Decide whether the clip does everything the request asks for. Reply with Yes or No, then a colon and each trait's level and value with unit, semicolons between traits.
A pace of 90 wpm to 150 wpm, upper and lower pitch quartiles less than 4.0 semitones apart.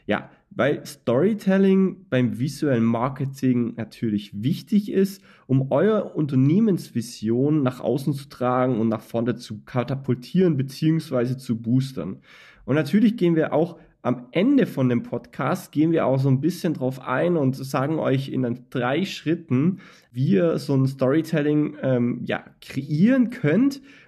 No: average, 140 wpm; average, 5.2 semitones